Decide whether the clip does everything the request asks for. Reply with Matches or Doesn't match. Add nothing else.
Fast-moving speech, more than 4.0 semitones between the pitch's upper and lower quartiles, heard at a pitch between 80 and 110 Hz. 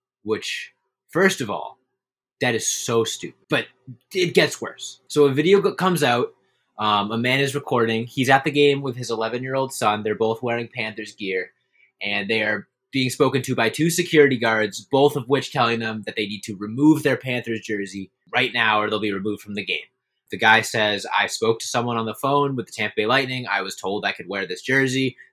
Doesn't match